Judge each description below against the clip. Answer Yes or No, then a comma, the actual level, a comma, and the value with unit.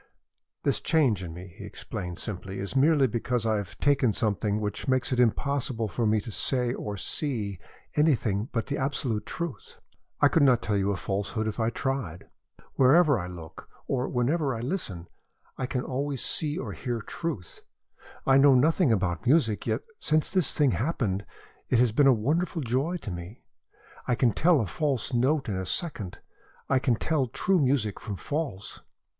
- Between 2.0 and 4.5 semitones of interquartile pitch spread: No, wide, 5.4 semitones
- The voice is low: Yes, low, 125 Hz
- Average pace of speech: Yes, average, 180 wpm